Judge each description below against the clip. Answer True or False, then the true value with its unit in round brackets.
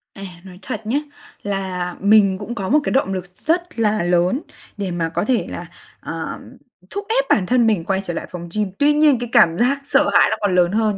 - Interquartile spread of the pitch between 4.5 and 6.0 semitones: True (5.5 semitones)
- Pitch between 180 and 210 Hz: True (205 Hz)